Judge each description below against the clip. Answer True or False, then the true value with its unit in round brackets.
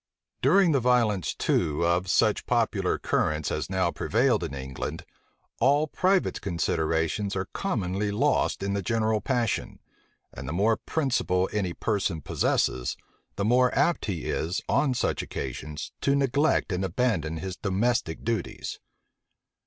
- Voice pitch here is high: False (100 Hz)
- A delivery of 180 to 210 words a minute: False (135 wpm)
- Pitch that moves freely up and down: True (6.4 semitones)